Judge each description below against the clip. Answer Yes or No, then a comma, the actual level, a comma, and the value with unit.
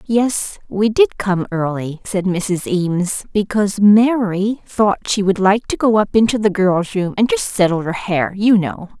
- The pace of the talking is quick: No, average, 185 wpm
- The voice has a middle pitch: No, high, 200 Hz